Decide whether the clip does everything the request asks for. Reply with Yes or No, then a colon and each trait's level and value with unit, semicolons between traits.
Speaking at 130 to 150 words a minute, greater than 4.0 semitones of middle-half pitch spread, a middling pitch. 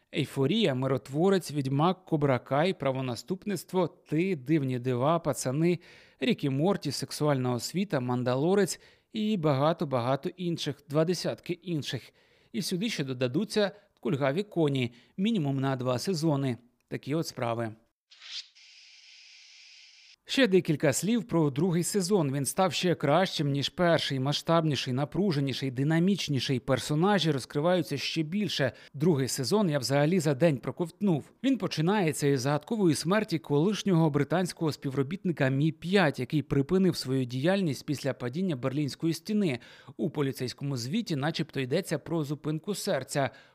No: average, 115 wpm; average, 5.0 semitones; medium, 155 Hz